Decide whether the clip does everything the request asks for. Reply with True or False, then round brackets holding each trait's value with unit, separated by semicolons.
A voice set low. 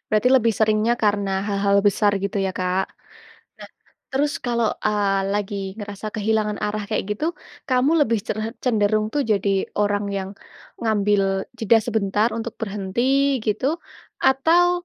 False (215 Hz)